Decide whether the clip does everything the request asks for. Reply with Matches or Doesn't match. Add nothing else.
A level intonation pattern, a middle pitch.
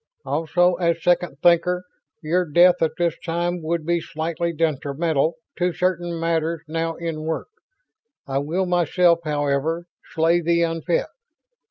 Matches